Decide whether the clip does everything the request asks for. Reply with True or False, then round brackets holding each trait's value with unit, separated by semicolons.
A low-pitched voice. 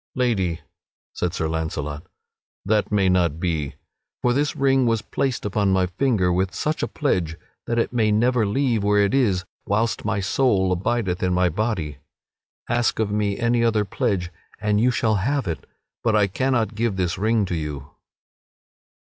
True (105 Hz)